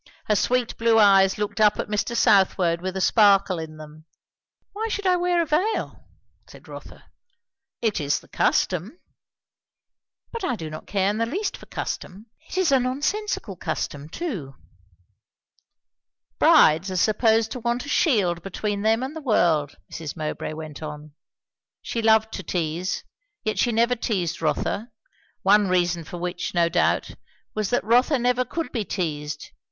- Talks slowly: No, average, 160 wpm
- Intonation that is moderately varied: No, wide, 6.0 semitones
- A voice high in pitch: Yes, high, 205 Hz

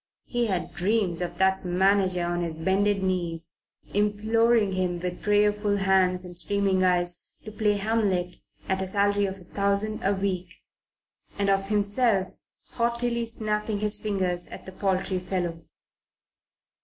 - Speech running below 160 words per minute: Yes, average, 145 wpm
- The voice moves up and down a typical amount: No, narrow, 2.3 semitones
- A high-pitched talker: Yes, high, 195 Hz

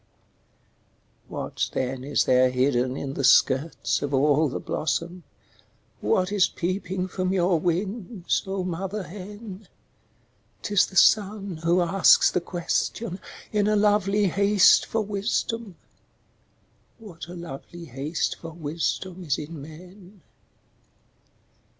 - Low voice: No, medium, 180 Hz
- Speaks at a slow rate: Yes, slow, 120 wpm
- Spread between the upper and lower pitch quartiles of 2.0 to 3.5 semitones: No, average, 4.0 semitones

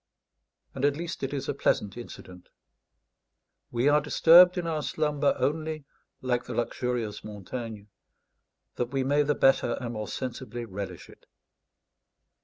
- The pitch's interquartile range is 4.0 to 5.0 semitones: Yes, average, 4.3 semitones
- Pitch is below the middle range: Yes, low, 130 Hz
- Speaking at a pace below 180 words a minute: Yes, average, 140 wpm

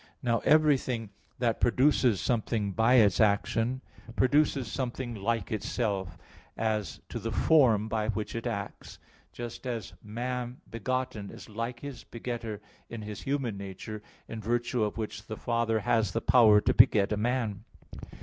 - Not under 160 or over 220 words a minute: No, average, 150 wpm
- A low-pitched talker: Yes, low, 115 Hz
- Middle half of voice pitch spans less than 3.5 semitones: Yes, average, 2.7 semitones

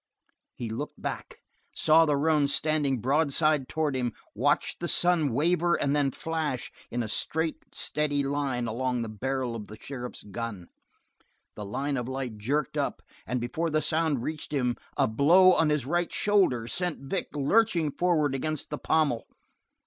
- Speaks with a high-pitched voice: No, medium, 145 Hz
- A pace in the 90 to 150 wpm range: No, average, 165 wpm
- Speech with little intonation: No, average, 4.3 semitones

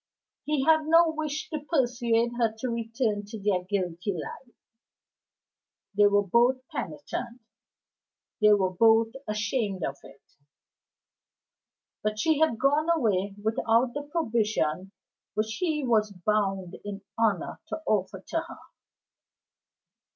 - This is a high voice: Yes, high, 225 Hz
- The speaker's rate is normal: No, slow, 120 wpm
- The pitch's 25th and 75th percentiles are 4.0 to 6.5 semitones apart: Yes, average, 4.8 semitones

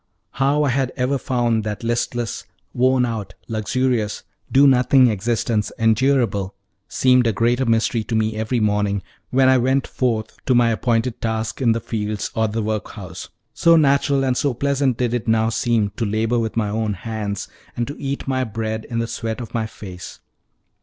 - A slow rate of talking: No, average, 175 wpm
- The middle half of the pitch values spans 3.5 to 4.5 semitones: No, average, 2.8 semitones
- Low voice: Yes, low, 115 Hz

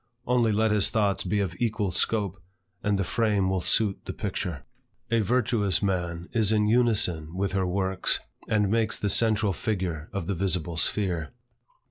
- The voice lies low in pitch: Yes, low, 100 Hz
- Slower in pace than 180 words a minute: Yes, average, 165 wpm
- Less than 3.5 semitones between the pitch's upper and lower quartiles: Yes, average, 3.0 semitones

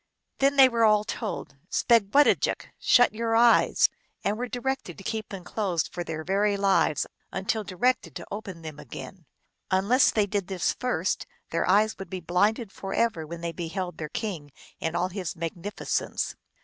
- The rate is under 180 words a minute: No, average, 185 wpm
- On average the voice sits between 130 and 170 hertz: No, high, 195 Hz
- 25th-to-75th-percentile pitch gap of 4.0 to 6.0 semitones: Yes, average, 4.3 semitones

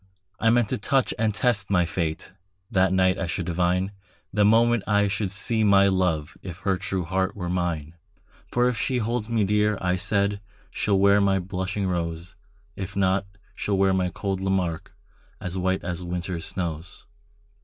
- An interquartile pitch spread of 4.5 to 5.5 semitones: No, narrow, 2.4 semitones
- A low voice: Yes, very low, 95 Hz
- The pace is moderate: Yes, average, 175 wpm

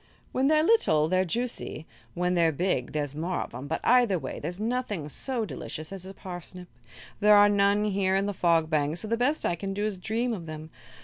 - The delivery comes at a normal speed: No, fast, 220 wpm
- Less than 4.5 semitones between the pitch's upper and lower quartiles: No, average, 4.8 semitones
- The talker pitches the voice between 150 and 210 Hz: Yes, high, 190 Hz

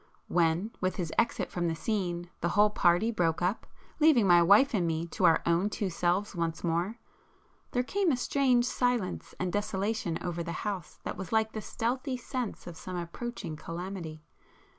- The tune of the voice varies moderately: Yes, average, 4.8 semitones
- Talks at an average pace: Yes, average, 180 wpm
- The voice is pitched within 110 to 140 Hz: No, medium, 185 Hz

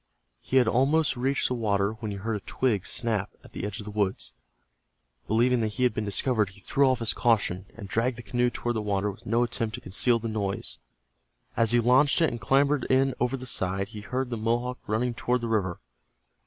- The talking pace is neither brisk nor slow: No, fast, 220 wpm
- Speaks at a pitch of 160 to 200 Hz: No, low, 115 Hz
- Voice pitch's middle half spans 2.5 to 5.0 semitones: Yes, average, 3.2 semitones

